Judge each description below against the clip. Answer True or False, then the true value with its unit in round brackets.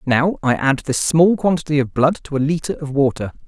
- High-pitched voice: False (145 Hz)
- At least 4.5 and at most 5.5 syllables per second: True (5.4 syllables/s)